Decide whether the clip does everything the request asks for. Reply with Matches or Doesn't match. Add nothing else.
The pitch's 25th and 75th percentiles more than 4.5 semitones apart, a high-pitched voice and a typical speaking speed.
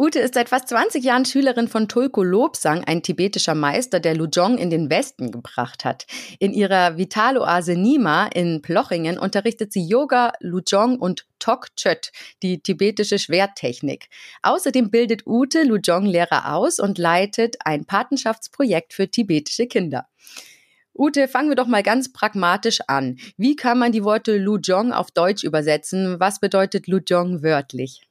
Matches